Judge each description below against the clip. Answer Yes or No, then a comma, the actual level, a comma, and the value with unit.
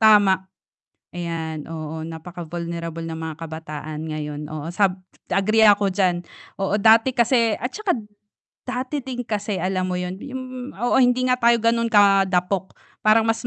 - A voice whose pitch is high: Yes, high, 195 Hz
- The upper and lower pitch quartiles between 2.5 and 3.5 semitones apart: No, wide, 5.6 semitones